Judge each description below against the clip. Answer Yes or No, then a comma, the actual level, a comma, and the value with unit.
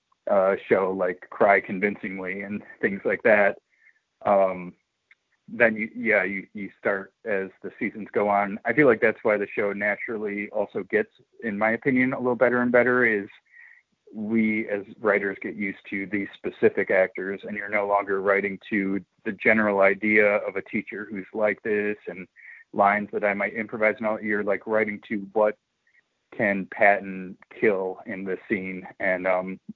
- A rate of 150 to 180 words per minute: Yes, average, 175 wpm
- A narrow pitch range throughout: Yes, narrow, 1.8 semitones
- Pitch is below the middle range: Yes, low, 100 Hz